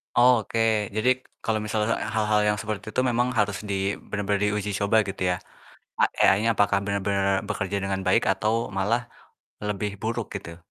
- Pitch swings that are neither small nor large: No, narrow, 2.1 semitones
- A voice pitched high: No, low, 105 Hz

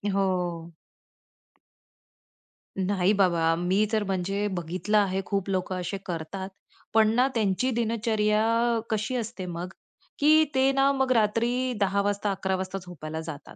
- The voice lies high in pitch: Yes, high, 200 Hz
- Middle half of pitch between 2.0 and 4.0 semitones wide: Yes, average, 3.7 semitones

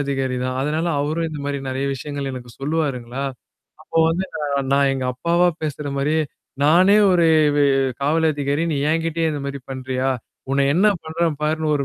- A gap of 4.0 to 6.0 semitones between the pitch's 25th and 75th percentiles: No, average, 2.9 semitones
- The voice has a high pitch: No, medium, 145 Hz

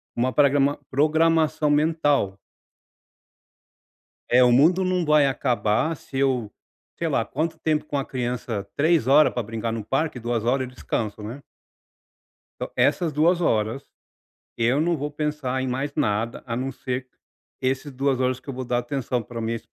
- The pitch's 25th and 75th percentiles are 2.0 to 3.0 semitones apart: No, average, 3.8 semitones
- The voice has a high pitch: No, low, 135 Hz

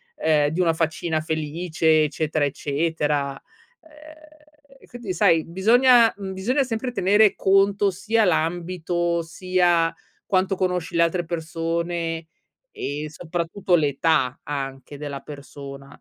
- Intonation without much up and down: No, average, 3.7 semitones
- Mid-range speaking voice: Yes, medium, 170 Hz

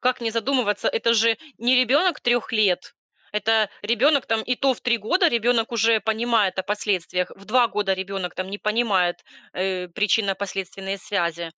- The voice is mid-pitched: No, high, 215 Hz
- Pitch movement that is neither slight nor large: Yes, average, 3.5 semitones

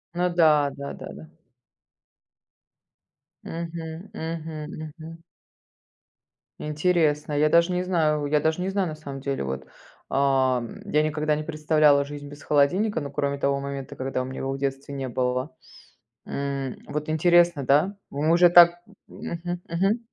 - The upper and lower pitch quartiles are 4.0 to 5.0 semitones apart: No, average, 3.3 semitones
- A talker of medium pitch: Yes, medium, 150 Hz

